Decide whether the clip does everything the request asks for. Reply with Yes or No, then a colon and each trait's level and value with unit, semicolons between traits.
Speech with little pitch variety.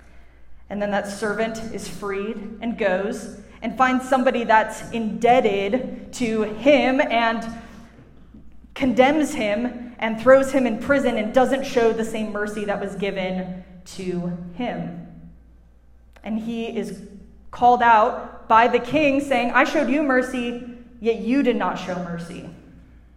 No: average, 3.5 semitones